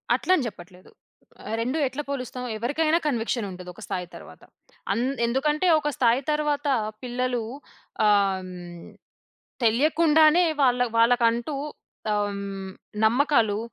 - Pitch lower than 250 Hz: Yes, high, 240 Hz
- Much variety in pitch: Yes, wide, 6.1 semitones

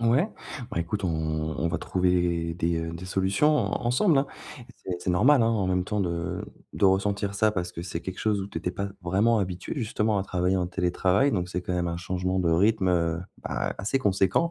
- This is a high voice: No, very low, 95 Hz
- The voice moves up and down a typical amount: Yes, average, 3.0 semitones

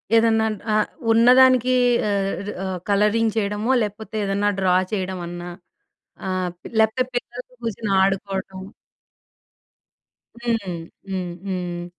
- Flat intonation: No, average, 3.2 semitones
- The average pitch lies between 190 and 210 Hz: Yes, high, 205 Hz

